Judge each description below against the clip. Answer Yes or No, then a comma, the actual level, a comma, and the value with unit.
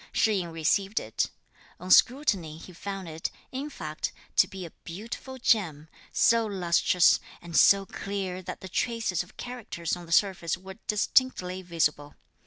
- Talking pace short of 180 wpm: Yes, average, 155 wpm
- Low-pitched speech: No, medium, 185 Hz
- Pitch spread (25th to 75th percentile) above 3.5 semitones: Yes, average, 3.9 semitones